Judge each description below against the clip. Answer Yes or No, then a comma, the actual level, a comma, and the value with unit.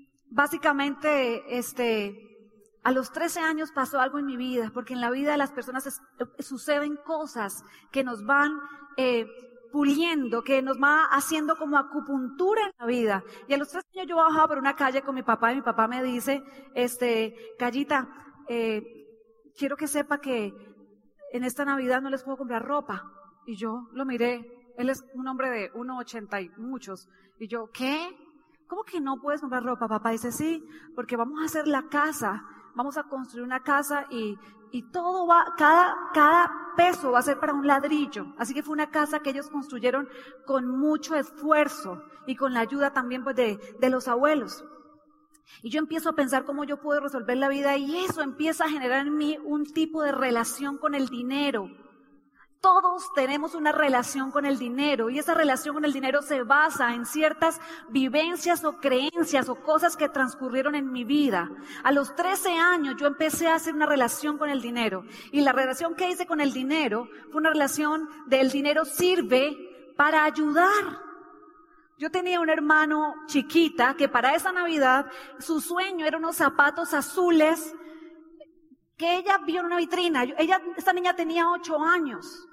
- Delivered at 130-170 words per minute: No, average, 180 wpm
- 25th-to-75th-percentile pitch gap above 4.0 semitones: No, average, 3.6 semitones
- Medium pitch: No, very high, 285 Hz